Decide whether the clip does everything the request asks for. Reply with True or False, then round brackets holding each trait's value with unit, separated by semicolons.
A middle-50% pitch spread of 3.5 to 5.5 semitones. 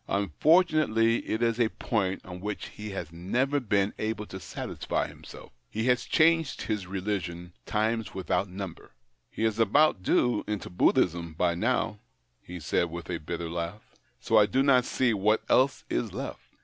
True (4.6 semitones)